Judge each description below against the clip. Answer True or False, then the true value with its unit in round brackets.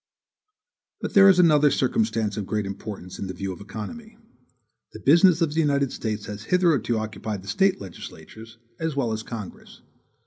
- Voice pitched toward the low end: True (115 Hz)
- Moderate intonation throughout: False (7.7 semitones)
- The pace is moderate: True (170 wpm)